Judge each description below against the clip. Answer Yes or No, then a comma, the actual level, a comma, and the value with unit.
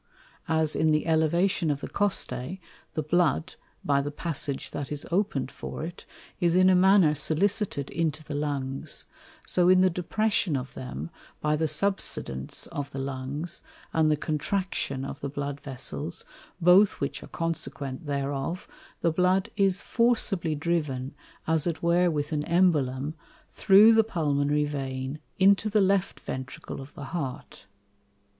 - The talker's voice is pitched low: No, medium, 155 Hz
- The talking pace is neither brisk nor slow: Yes, average, 150 wpm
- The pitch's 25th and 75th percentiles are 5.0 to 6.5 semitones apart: No, average, 4.3 semitones